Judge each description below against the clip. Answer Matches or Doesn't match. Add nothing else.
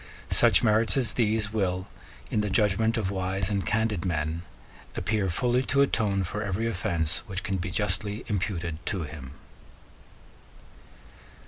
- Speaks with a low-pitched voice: Matches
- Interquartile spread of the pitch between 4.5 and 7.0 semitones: Doesn't match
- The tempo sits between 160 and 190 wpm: Doesn't match